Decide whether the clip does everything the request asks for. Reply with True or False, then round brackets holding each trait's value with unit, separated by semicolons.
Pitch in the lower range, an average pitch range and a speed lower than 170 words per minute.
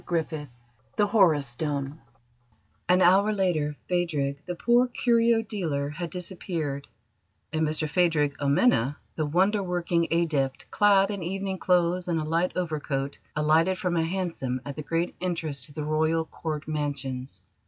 False (165 Hz; 3.7 semitones; 150 wpm)